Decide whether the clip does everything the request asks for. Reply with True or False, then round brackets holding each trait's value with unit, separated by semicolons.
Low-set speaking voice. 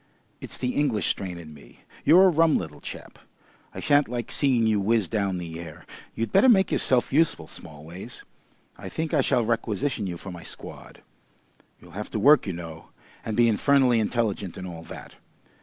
True (110 Hz)